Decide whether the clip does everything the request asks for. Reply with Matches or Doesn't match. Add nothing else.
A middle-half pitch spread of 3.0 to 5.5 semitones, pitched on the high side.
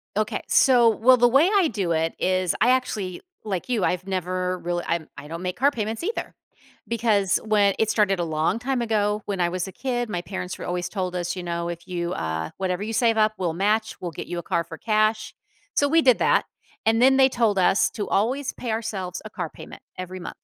Matches